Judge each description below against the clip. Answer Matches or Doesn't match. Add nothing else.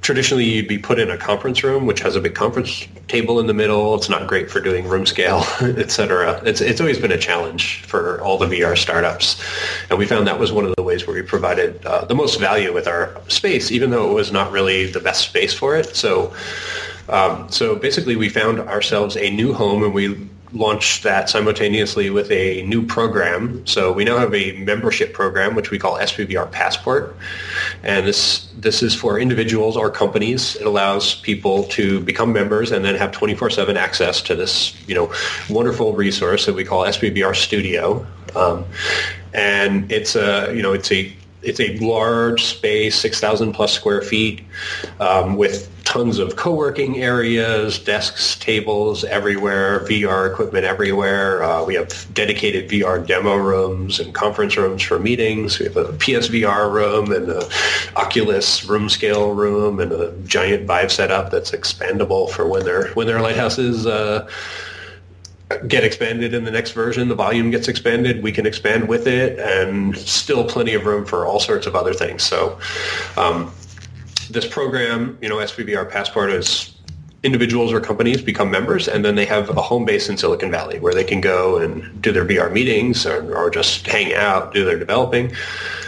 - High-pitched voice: Doesn't match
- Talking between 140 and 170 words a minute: Doesn't match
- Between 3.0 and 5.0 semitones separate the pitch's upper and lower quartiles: Doesn't match